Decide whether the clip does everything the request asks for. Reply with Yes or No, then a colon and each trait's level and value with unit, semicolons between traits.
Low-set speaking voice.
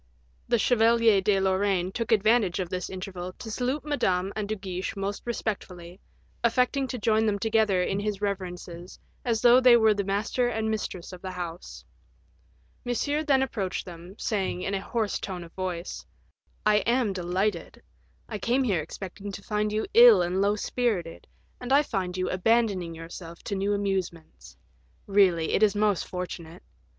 No: high, 200 Hz